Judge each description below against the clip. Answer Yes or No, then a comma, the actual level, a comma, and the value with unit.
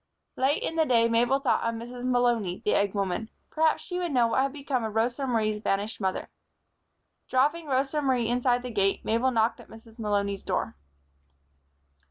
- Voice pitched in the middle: No, high, 240 Hz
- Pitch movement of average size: Yes, average, 3.3 semitones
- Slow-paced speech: No, average, 180 wpm